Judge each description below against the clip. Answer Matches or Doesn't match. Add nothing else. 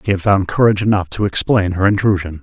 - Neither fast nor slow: Doesn't match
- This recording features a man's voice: Matches